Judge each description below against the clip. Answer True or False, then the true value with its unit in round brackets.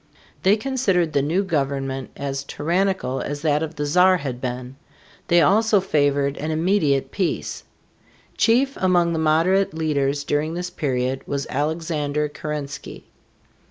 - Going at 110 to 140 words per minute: True (135 wpm)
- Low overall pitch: False (155 Hz)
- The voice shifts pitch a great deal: False (4.3 semitones)